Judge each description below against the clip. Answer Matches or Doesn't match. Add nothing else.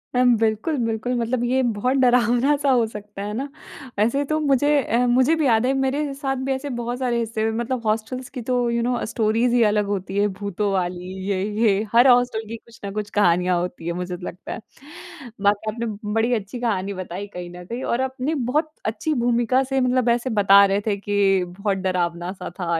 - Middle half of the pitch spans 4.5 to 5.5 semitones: Doesn't match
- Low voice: Doesn't match